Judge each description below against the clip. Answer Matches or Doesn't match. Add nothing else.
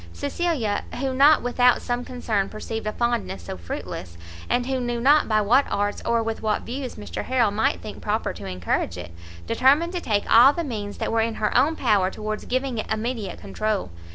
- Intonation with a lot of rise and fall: Doesn't match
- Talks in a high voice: Matches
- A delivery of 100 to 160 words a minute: Doesn't match